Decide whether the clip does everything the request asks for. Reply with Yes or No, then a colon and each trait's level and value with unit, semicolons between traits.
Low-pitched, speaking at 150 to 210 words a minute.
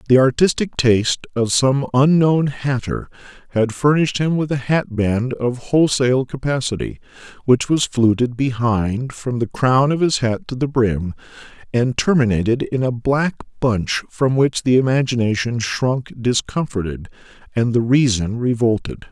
No: low, 125 Hz; average, 140 wpm